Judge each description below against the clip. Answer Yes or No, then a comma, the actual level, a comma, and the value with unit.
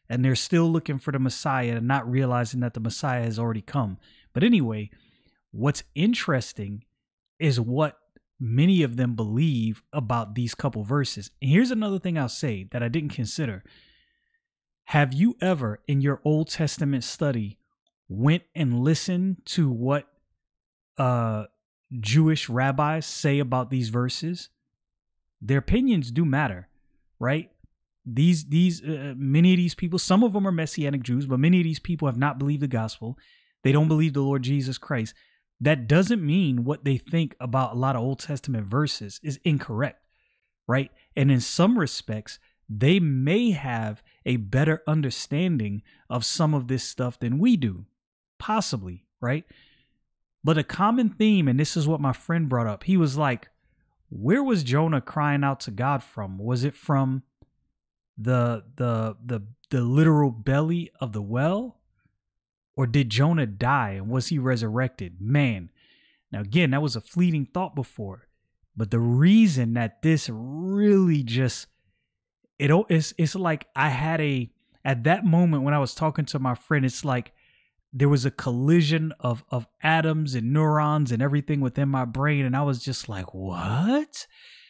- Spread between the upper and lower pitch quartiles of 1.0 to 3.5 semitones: No, average, 4.6 semitones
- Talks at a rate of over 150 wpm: Yes, average, 165 wpm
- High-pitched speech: No, medium, 140 Hz